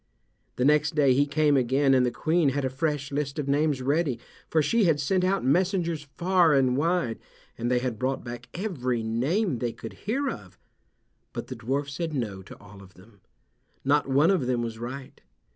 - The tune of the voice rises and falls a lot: No, average, 4.3 semitones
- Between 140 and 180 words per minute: No, average, 195 wpm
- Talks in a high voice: No, medium, 140 Hz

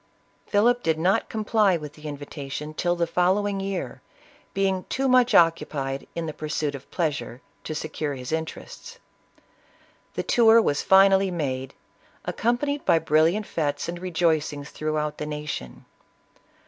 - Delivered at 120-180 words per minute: Yes, average, 140 wpm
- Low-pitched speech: No, medium, 165 Hz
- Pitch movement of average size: Yes, average, 4.7 semitones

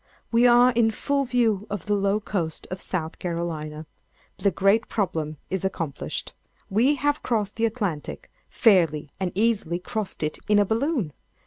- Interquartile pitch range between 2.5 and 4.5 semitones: No, average, 5.1 semitones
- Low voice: No, high, 200 Hz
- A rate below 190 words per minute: Yes, average, 150 wpm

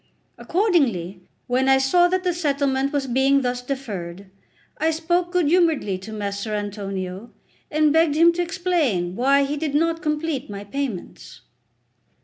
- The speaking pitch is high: Yes, very high, 275 Hz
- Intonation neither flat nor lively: No, wide, 7.9 semitones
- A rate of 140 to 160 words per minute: Yes, average, 145 wpm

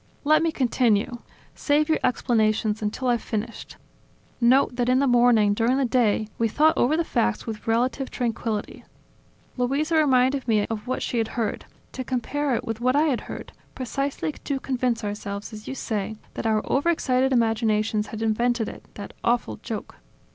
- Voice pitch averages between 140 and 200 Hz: No, high, 240 Hz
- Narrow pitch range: No, average, 3.3 semitones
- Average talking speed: Yes, average, 170 wpm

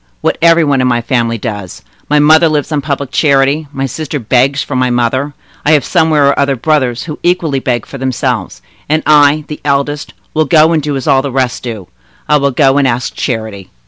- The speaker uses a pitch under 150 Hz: Yes, medium, 140 Hz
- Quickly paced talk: Yes, fast, 210 wpm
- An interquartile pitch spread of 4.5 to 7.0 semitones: No, average, 3.3 semitones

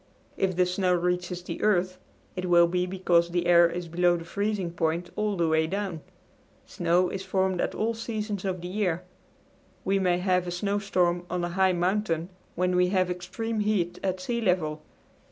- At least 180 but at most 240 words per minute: Yes, average, 185 wpm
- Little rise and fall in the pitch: Yes, narrow, 1.7 semitones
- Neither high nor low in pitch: Yes, medium, 180 Hz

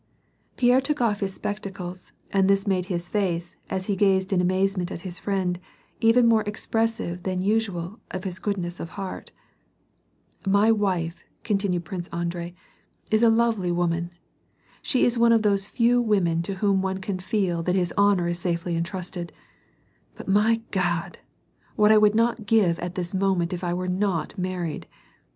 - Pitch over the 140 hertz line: Yes, high, 190 Hz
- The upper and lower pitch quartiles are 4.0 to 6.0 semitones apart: No, average, 3.0 semitones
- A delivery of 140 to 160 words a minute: No, average, 175 wpm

